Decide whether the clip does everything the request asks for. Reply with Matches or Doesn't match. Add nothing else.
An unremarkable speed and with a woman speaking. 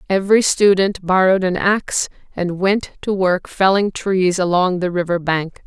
Matches